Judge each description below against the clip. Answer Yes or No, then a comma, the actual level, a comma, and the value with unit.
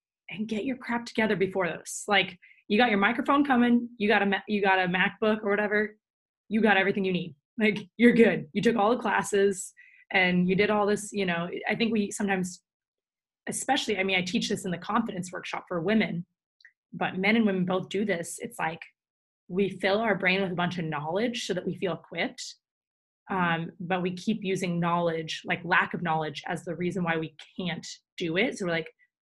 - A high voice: Yes, high, 200 Hz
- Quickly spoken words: Yes, fast, 210 wpm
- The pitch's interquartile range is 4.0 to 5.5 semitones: No, average, 3.1 semitones